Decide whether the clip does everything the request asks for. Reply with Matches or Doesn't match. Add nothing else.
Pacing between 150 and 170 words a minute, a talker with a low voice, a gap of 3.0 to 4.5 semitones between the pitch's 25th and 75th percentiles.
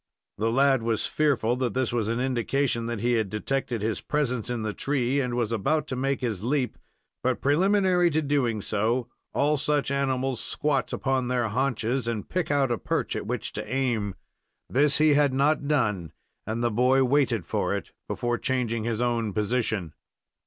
Doesn't match